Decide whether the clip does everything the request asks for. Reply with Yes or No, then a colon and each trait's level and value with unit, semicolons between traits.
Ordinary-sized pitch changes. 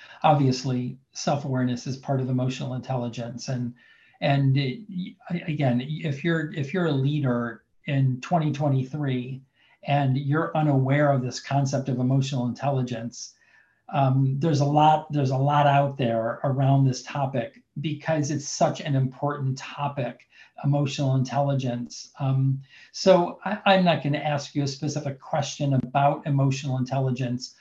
No: narrow, 2.2 semitones